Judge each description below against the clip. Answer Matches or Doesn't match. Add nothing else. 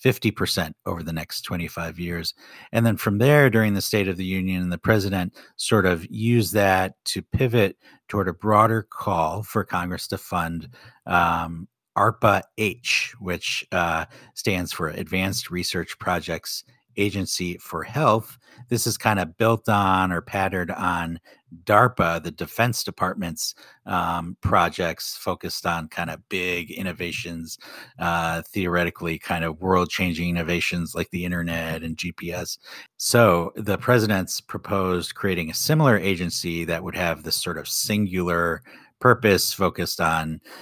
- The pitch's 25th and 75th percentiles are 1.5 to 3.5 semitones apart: Doesn't match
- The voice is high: Doesn't match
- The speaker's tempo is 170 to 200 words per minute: Doesn't match